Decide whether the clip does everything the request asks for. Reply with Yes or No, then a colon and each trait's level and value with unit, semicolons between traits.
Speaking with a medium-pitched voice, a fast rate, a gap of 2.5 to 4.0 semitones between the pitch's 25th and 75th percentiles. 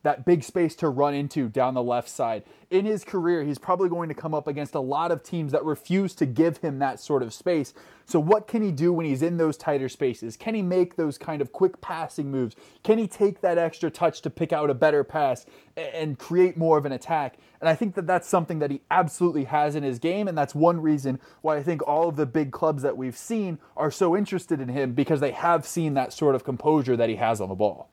Yes: medium, 160 Hz; fast, 255 wpm; average, 3.5 semitones